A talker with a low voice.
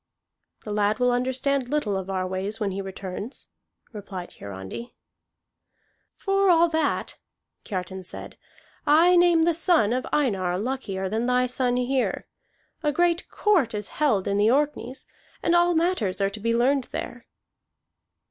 No: high, 245 Hz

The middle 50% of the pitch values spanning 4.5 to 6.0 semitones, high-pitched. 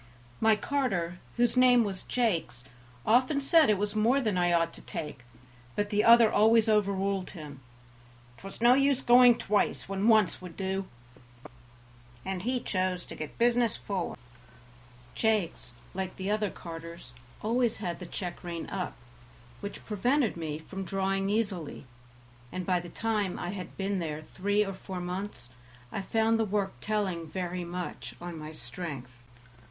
No: average, 4.0 semitones; high, 195 Hz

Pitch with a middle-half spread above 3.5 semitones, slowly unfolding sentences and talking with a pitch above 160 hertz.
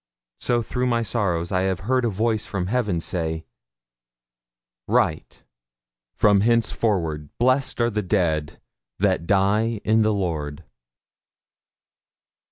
No: average, 5.0 semitones; slow, 115 wpm; low, 100 Hz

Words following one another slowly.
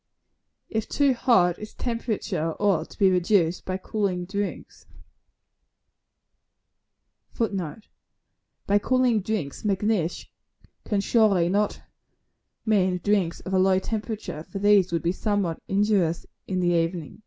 Yes: slow, 120 wpm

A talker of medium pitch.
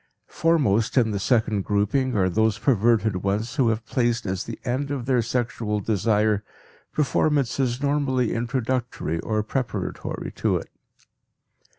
No: low, 115 Hz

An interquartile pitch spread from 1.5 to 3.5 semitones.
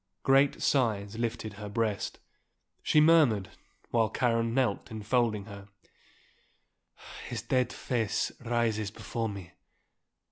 Yes: average, 2.7 semitones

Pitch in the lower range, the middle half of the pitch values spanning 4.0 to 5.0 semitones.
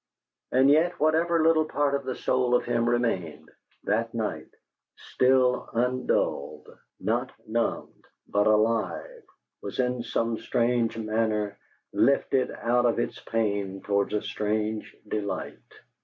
No: low, 115 Hz; average, 3.2 semitones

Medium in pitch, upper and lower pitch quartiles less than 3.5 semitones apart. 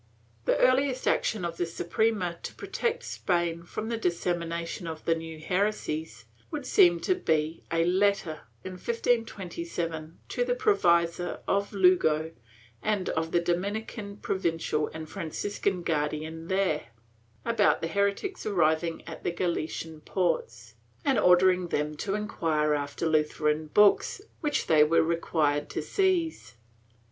No: medium, 170 Hz; average, 4.1 semitones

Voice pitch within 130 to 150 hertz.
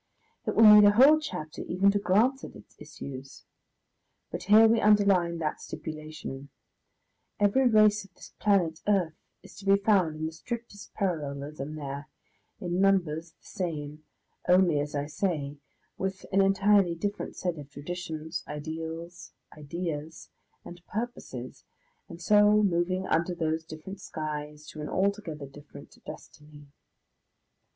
No: medium, 170 Hz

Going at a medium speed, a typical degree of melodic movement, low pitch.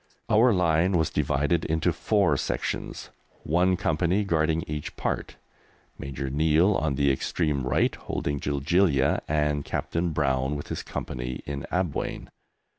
No: slow, 130 wpm; average, 3.5 semitones; very low, 75 Hz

